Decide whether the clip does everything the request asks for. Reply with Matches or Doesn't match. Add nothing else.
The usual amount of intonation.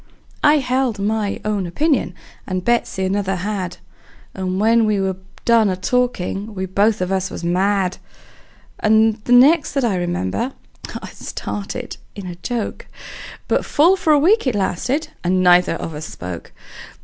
Matches